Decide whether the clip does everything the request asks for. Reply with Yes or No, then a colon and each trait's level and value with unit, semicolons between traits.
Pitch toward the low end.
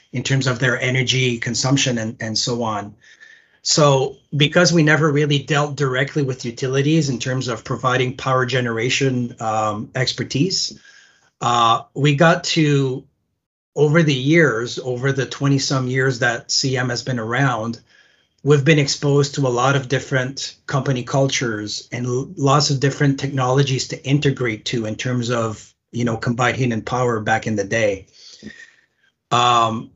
Yes: low, 130 Hz